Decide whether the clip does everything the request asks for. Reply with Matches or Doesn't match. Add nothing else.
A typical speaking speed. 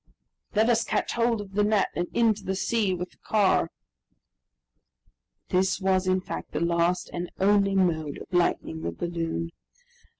Matches